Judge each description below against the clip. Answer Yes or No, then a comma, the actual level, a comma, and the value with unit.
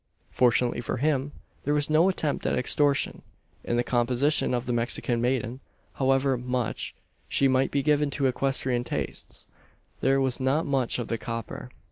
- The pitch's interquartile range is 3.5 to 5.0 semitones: No, narrow, 2.6 semitones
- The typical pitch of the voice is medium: No, low, 130 Hz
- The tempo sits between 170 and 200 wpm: No, average, 160 wpm